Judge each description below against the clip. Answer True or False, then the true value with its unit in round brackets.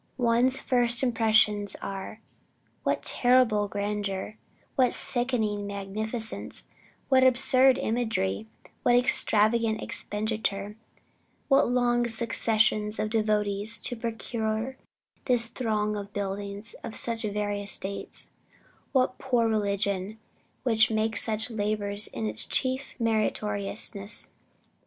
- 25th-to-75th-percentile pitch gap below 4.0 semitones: True (2.6 semitones)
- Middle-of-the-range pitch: False (220 Hz)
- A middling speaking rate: False (100 wpm)